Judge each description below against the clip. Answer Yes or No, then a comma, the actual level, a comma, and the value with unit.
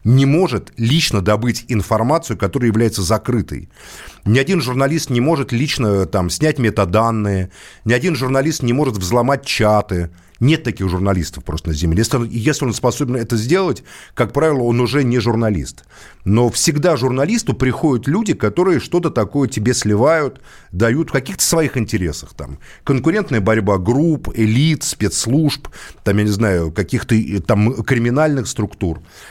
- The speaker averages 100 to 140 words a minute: No, average, 150 wpm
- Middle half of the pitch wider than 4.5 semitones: Yes, average, 5.0 semitones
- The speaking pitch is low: Yes, low, 115 Hz